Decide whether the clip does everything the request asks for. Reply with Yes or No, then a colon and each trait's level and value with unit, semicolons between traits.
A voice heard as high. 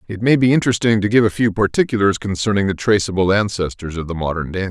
No: low, 100 Hz